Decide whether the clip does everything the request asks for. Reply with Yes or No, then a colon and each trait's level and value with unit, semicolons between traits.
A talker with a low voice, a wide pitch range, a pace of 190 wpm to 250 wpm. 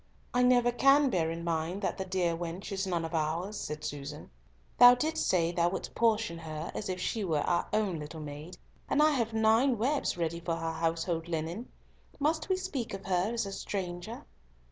No: medium, 185 Hz; wide, 5.7 semitones; average, 200 wpm